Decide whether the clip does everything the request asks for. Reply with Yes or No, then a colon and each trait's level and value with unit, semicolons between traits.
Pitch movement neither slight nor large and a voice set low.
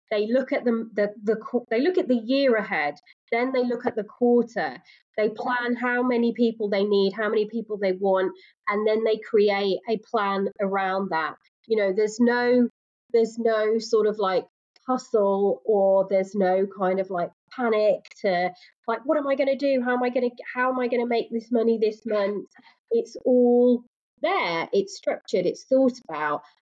No: average, 3.6 semitones; high, 225 Hz